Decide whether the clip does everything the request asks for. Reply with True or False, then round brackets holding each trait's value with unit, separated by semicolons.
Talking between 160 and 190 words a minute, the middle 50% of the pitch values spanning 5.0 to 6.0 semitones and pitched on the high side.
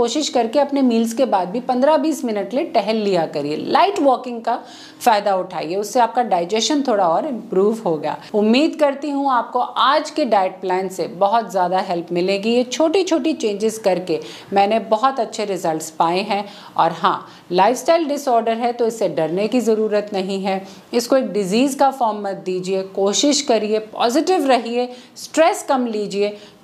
True (170 wpm; 5.4 semitones; 220 Hz)